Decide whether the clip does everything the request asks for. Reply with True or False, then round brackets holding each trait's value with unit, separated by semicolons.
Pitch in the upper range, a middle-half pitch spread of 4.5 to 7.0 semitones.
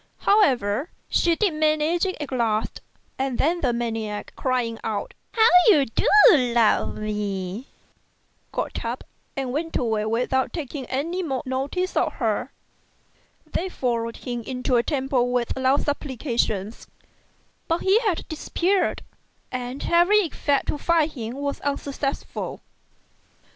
True (265 Hz; 5.1 semitones)